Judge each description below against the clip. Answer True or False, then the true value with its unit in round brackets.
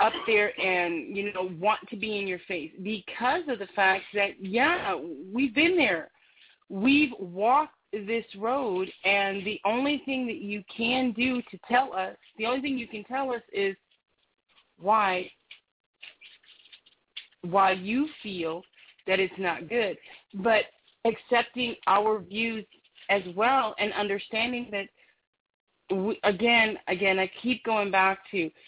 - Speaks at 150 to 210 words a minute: False (140 wpm)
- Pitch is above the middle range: True (210 Hz)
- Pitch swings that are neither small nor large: True (3.7 semitones)